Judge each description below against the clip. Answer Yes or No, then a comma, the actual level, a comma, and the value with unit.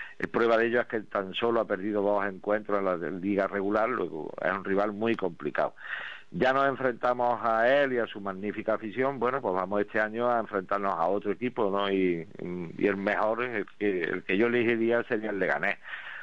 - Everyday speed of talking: No, fast, 205 wpm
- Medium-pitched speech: No, low, 105 Hz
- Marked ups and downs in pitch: No, average, 2.9 semitones